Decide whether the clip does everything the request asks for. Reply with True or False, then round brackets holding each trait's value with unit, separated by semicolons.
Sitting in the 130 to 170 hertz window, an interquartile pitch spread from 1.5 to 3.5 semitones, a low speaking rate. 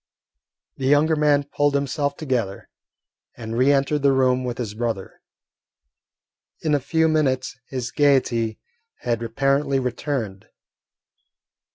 True (135 Hz; 3.2 semitones; 115 wpm)